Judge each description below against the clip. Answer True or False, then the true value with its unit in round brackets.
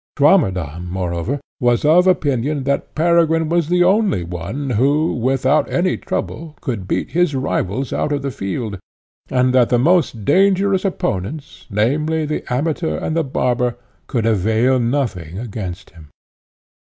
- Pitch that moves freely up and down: True (6.4 semitones)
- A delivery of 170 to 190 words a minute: False (140 wpm)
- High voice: False (130 Hz)